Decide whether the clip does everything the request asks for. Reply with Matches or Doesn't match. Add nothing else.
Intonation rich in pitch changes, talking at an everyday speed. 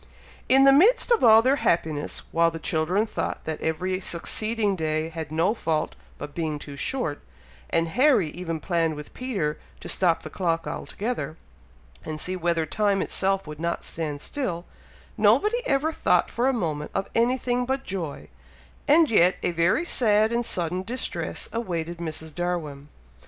Matches